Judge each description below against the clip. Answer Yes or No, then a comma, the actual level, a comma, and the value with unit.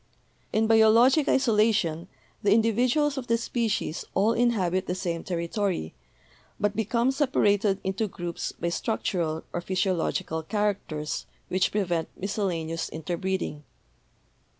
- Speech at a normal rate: No, slow, 115 wpm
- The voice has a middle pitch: No, high, 200 Hz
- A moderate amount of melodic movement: Yes, average, 4.6 semitones